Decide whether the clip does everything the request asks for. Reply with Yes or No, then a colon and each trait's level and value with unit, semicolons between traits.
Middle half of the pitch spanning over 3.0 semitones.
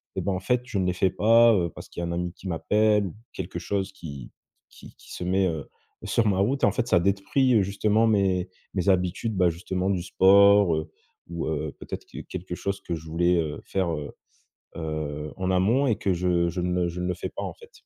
No: average, 2.7 semitones